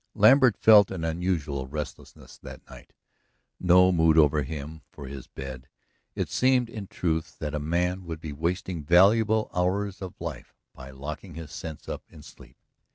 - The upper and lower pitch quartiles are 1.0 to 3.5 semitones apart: No, average, 4.1 semitones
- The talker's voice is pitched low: Yes, very low, 85 Hz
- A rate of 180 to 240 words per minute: No, average, 160 wpm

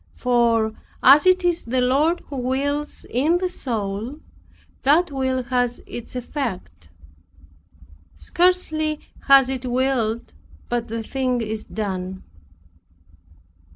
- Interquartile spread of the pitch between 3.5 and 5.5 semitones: Yes, average, 4.1 semitones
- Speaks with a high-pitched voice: Yes, very high, 255 Hz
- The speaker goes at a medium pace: No, slow, 110 wpm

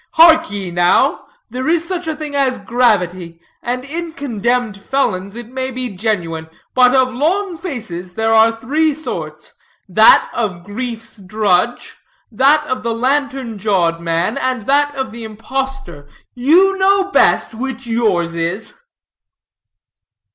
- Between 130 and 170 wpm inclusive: Yes, average, 140 wpm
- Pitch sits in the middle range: No, high, 240 Hz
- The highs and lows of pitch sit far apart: Yes, wide, 5.7 semitones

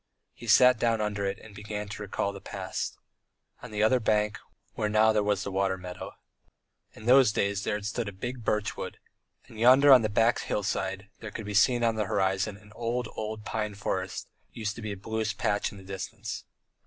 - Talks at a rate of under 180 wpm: No, fast, 205 wpm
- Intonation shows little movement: Yes, narrow, 1.9 semitones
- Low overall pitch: Yes, low, 105 Hz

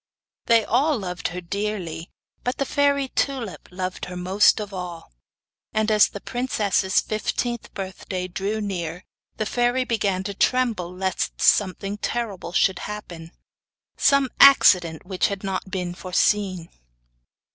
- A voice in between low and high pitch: No, high, 200 Hz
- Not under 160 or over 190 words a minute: No, slow, 135 wpm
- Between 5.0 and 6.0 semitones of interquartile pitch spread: No, average, 3.8 semitones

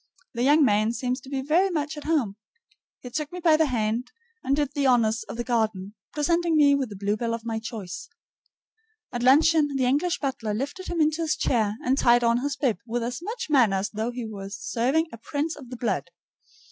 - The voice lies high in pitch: Yes, very high, 255 Hz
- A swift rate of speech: Yes, fast, 215 wpm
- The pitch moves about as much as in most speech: Yes, average, 4.7 semitones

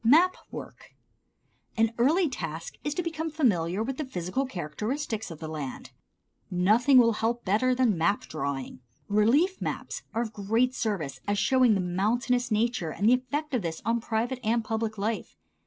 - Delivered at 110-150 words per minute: No, average, 170 wpm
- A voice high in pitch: Yes, high, 225 Hz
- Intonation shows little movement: No, average, 4.8 semitones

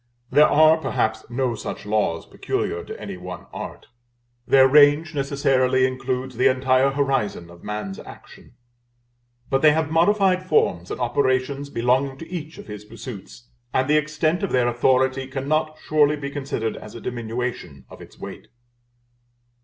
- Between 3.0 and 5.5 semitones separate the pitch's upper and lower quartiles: Yes, average, 3.7 semitones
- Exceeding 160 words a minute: No, average, 155 wpm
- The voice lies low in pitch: Yes, low, 130 Hz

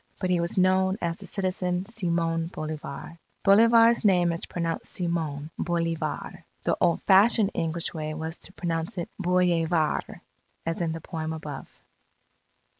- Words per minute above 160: No, average, 140 wpm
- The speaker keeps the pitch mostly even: Yes, narrow, 2.3 semitones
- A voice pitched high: No, medium, 170 Hz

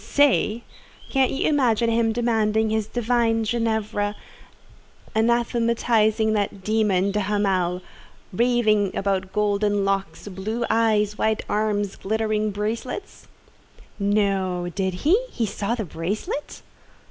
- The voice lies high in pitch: Yes, high, 215 Hz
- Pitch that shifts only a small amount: Yes, narrow, 2.3 semitones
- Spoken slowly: Yes, slow, 105 wpm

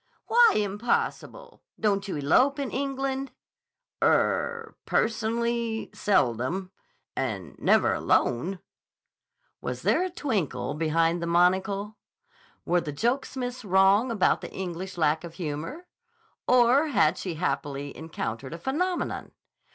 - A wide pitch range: Yes, wide, 7.4 semitones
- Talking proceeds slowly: Yes, slow, 110 wpm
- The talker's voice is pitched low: No, high, 195 Hz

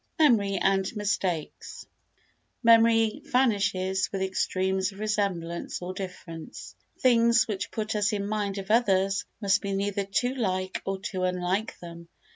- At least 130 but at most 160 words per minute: Yes, slow, 135 wpm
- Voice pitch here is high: Yes, high, 195 Hz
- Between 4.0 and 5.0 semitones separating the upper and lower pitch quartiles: No, narrow, 2.4 semitones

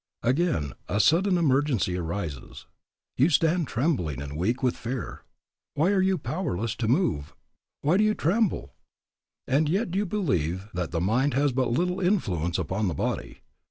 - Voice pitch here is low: Yes, low, 130 Hz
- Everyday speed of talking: Yes, average, 160 wpm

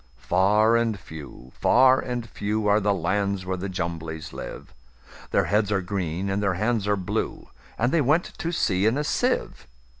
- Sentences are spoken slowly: No, average, 160 wpm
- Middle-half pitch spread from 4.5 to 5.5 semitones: No, average, 3.7 semitones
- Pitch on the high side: No, low, 100 Hz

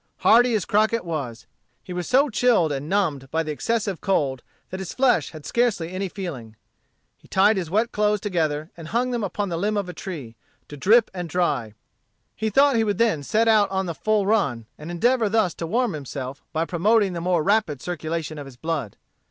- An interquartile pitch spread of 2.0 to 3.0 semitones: No, wide, 5.6 semitones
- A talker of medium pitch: Yes, medium, 180 Hz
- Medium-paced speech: No, fast, 210 wpm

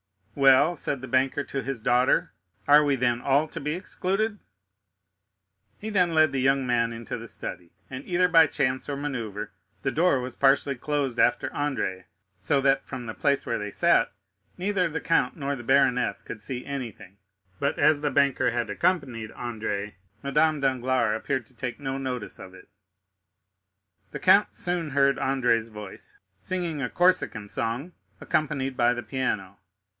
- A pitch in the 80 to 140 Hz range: Yes, low, 135 Hz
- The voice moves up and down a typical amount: Yes, average, 3.4 semitones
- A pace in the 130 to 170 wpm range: Yes, average, 165 wpm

